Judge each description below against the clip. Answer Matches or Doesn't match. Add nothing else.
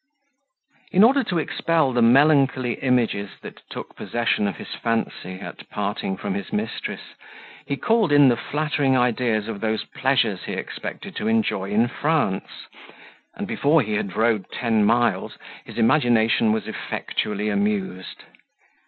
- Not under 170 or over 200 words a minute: Doesn't match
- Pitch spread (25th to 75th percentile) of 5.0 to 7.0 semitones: Matches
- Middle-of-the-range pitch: Doesn't match